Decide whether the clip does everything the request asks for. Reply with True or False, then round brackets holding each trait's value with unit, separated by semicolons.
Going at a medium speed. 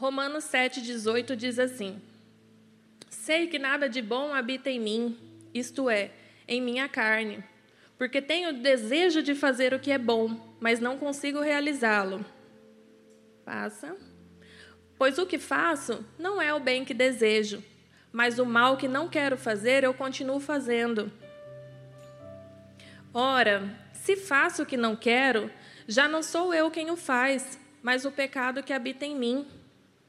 True (145 wpm)